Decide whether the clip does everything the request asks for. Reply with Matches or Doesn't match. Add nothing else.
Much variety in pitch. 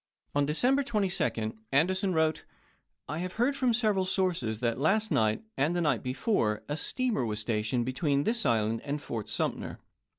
Matches